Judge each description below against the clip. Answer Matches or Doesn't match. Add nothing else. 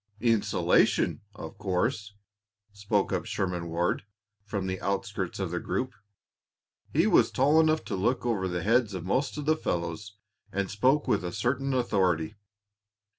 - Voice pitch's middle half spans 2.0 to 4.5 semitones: Doesn't match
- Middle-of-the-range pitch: Doesn't match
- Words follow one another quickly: Doesn't match